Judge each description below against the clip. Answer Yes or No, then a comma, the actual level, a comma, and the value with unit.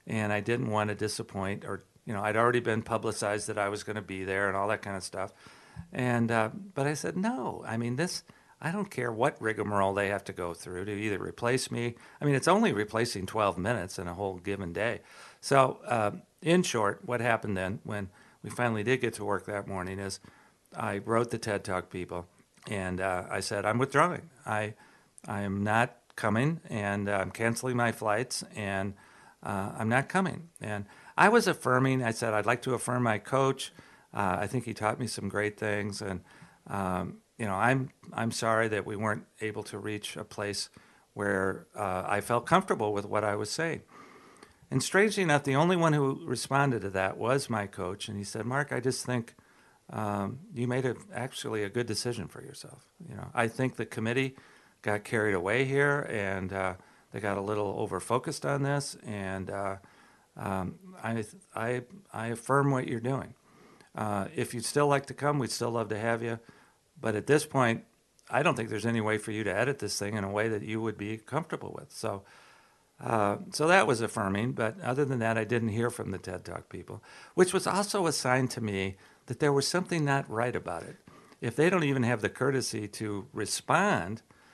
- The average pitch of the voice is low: Yes, low, 110 Hz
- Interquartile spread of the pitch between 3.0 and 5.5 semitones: Yes, average, 4.1 semitones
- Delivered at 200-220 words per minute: Yes, fast, 205 wpm